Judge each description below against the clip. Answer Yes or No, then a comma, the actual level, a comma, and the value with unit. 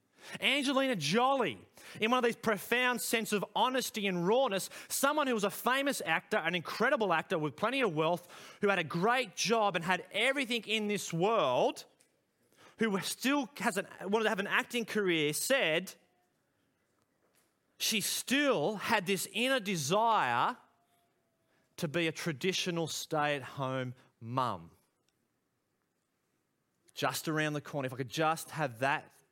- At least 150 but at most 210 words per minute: No, average, 140 wpm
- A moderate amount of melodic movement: No, wide, 6.8 semitones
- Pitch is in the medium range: No, high, 200 Hz